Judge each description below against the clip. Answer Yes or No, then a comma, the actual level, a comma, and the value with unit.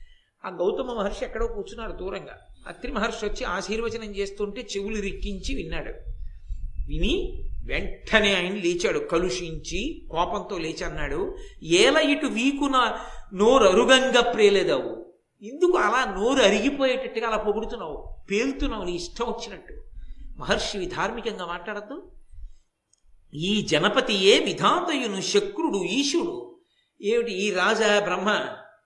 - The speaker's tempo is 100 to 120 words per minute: Yes, average, 105 wpm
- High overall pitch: Yes, high, 220 Hz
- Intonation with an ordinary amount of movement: No, wide, 6.0 semitones